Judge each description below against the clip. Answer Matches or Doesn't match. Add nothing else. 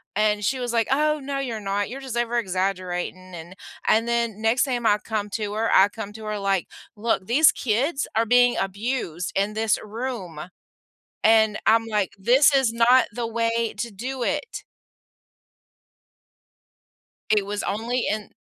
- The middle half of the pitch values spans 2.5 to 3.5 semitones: Matches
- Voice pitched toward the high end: Matches